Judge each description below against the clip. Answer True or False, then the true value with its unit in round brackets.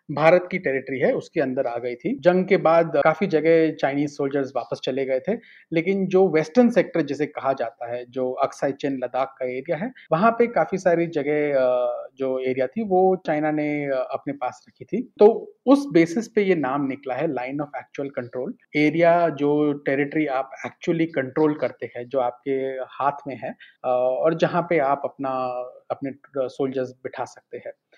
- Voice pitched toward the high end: False (145 Hz)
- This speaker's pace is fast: False (180 wpm)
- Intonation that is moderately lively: True (4.4 semitones)